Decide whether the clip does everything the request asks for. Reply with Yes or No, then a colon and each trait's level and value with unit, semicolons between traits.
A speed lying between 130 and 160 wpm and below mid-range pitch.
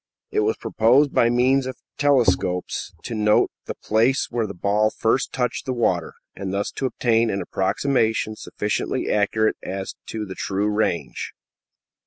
Yes: average, 155 wpm; low, 110 Hz